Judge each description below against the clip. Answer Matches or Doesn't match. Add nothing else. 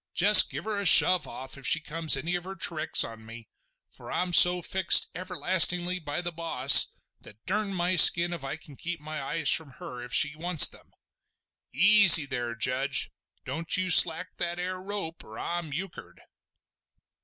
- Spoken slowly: Doesn't match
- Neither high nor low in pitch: Matches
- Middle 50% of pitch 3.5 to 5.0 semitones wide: Matches